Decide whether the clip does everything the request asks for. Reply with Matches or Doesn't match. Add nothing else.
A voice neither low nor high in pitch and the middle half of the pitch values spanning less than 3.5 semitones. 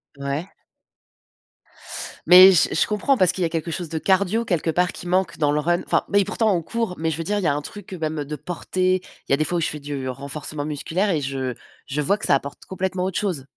Doesn't match